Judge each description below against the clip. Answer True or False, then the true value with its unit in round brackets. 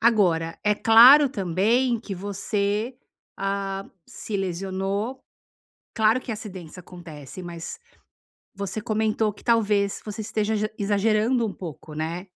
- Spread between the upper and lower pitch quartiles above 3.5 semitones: False (2.8 semitones)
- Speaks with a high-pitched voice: True (205 Hz)